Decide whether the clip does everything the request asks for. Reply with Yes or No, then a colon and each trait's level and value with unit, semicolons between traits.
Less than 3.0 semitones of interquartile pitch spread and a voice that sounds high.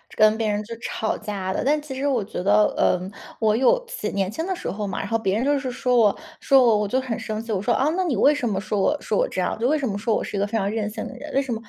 No: average, 4.5 semitones; high, 225 Hz